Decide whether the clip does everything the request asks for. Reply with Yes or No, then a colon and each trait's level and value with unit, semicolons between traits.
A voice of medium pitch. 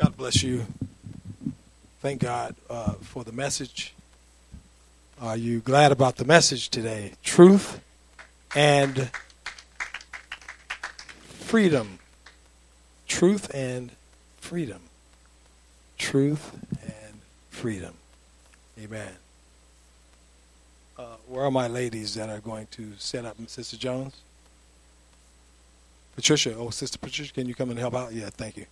No: low, 110 Hz